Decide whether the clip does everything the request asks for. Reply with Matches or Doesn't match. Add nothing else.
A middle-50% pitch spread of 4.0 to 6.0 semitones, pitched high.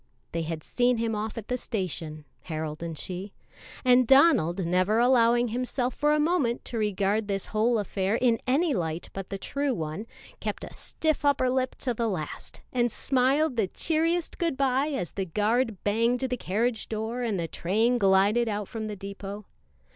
Matches